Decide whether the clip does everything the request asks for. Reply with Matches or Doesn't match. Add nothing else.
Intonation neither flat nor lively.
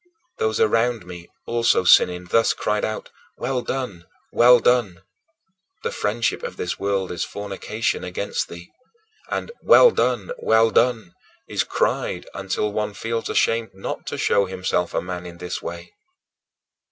Matches